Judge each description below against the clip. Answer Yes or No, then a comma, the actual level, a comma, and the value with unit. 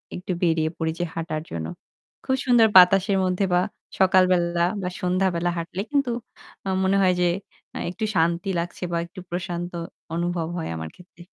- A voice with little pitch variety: Yes, narrow, 1.8 semitones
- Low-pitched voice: No, medium, 180 Hz